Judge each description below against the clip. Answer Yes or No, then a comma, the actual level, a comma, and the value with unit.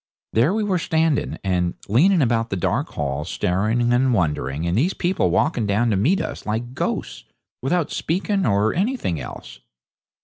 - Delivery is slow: No, average, 165 wpm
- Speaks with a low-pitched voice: Yes, low, 120 Hz